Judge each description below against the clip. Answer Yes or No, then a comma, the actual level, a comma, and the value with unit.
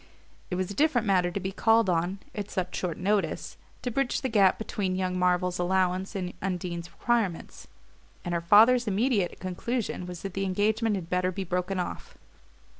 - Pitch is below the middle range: No, high, 190 Hz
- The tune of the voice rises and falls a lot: No, average, 2.7 semitones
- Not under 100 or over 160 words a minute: No, average, 180 wpm